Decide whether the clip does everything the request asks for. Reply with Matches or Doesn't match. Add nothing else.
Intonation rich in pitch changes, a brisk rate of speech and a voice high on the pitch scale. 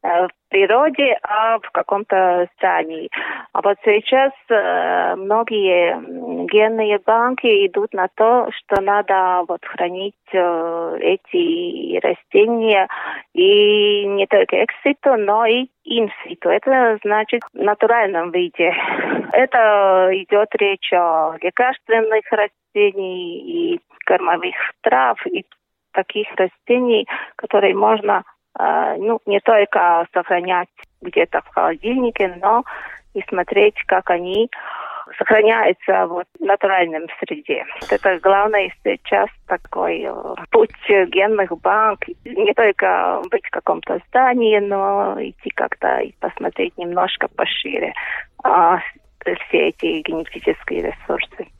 Doesn't match